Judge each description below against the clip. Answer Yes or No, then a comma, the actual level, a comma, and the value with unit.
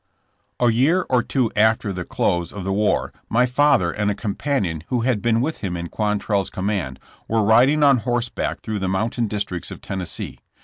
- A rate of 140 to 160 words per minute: No, average, 185 wpm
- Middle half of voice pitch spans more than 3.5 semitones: Yes, average, 4.0 semitones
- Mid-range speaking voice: No, low, 110 Hz